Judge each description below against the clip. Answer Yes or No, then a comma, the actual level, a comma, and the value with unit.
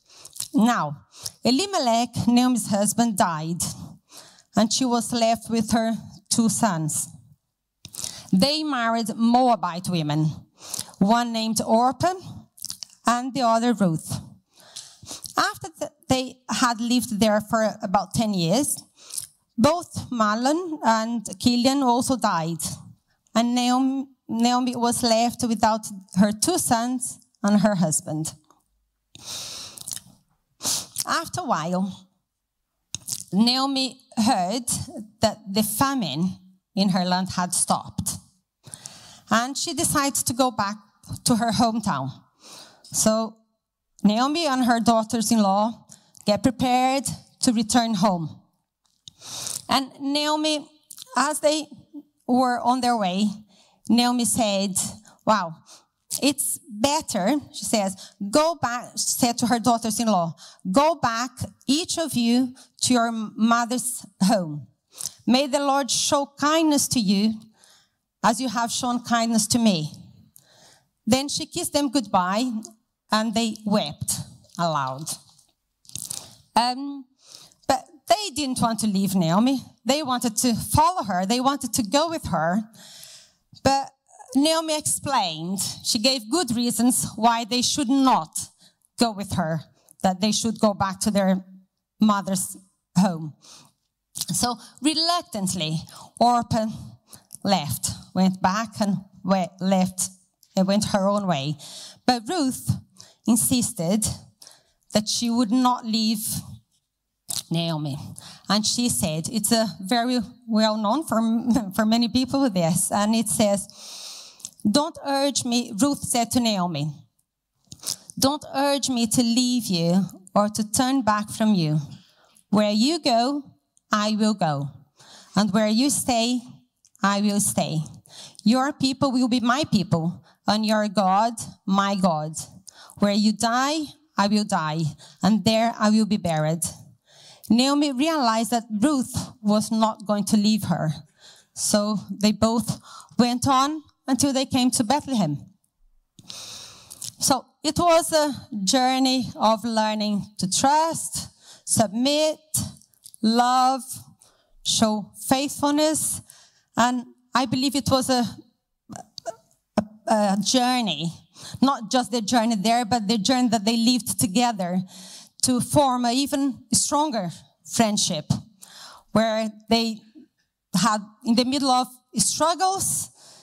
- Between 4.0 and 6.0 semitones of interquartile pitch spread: Yes, average, 4.4 semitones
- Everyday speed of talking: No, slow, 120 wpm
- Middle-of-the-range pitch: No, high, 225 Hz